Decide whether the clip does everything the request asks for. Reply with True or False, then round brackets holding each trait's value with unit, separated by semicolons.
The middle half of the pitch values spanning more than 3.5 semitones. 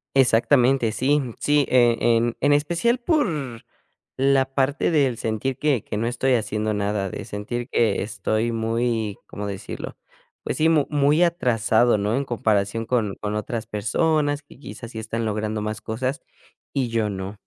True (4.2 semitones)